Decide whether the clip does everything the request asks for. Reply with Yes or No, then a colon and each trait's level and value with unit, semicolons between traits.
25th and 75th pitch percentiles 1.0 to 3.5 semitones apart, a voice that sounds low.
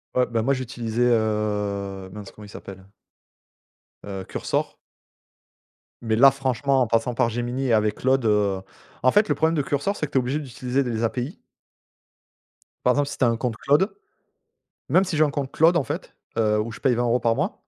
No: average, 3.9 semitones; low, 120 Hz